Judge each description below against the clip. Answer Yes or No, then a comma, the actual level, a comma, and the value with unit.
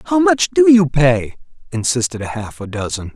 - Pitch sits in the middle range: Yes, medium, 150 Hz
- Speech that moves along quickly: No, average, 170 wpm